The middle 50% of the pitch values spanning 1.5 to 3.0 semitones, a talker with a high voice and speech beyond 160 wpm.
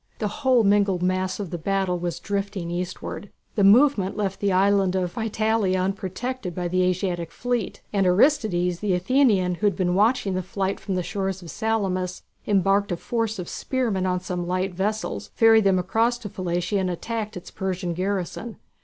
Yes: average, 2.7 semitones; high, 195 Hz; average, 180 wpm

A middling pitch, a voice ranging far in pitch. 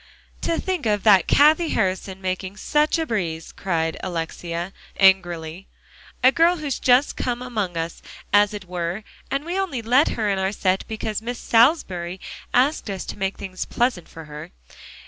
No: high, 205 Hz; wide, 5.7 semitones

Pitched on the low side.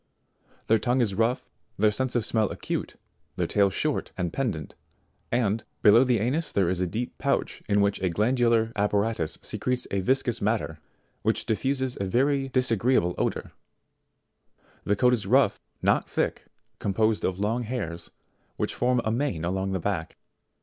Yes: low, 110 Hz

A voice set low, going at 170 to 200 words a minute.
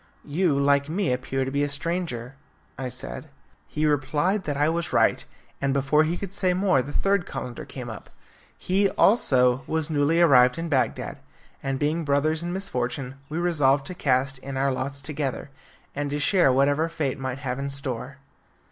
No: medium, 145 Hz; average, 180 wpm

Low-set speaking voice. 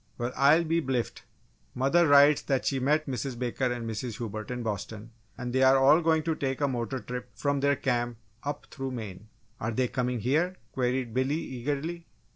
Yes: low, 130 Hz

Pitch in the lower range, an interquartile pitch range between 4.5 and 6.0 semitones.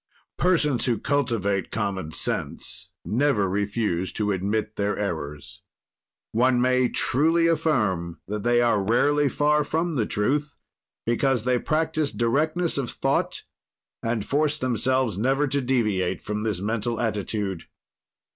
Yes: low, 120 Hz; wide, 5.6 semitones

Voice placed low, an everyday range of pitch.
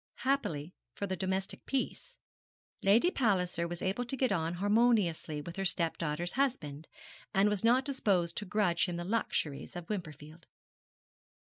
No: high, 190 Hz; average, 5.0 semitones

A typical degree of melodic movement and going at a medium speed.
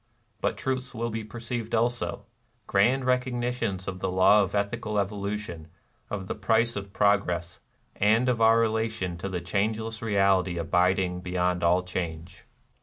Yes: average, 3.5 semitones; average, 155 wpm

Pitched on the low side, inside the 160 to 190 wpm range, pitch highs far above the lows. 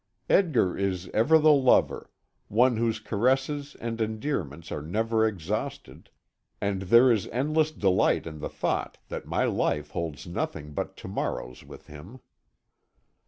No: low, 110 Hz; average, 140 wpm; wide, 6.9 semitones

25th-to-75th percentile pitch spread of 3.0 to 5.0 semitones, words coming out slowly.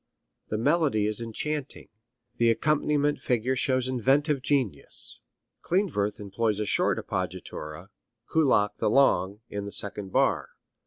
No: wide, 5.6 semitones; slow, 120 wpm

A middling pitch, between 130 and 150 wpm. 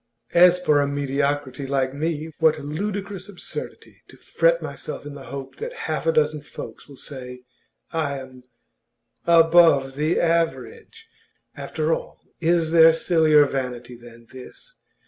Yes: medium, 150 Hz; average, 140 wpm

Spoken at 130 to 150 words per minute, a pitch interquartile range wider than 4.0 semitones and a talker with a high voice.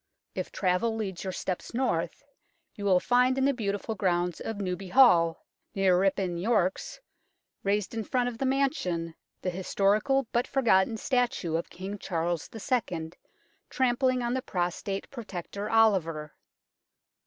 Yes: average, 140 wpm; average, 5.1 semitones; high, 200 Hz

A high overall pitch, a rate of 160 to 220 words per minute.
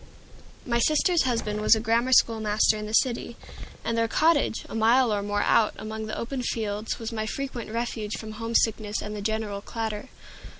Yes: high, 225 Hz; average, 185 wpm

